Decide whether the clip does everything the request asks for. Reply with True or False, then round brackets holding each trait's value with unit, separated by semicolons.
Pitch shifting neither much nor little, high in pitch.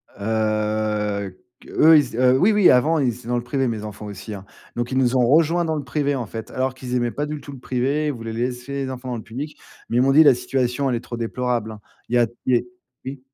False (3.3 semitones; 125 Hz)